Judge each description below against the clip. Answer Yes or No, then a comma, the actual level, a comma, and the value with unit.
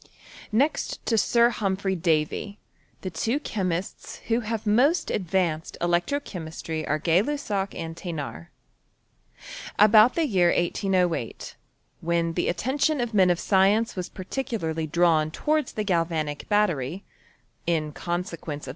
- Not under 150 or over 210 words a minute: No, slow, 135 wpm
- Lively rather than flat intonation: No, average, 4.7 semitones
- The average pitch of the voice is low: No, medium, 185 Hz